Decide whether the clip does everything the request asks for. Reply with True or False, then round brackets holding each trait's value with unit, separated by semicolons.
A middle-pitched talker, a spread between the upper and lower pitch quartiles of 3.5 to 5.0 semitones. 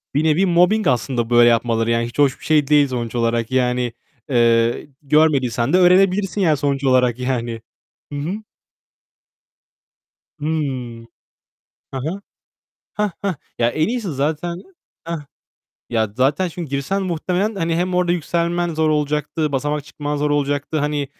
False (145 Hz; 5.4 semitones)